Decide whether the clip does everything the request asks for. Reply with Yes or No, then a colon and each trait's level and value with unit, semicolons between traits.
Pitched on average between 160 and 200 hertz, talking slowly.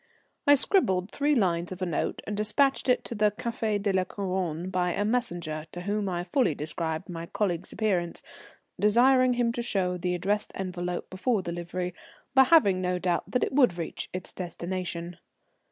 No: medium, 185 Hz; average, 175 wpm